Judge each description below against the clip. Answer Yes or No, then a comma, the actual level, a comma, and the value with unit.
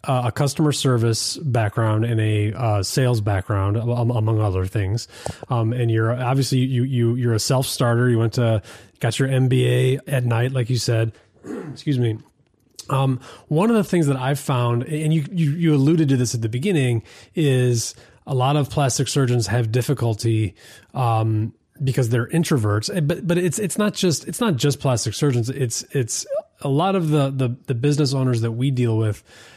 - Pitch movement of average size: Yes, average, 3.8 semitones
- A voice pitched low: Yes, low, 125 Hz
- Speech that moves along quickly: No, average, 190 wpm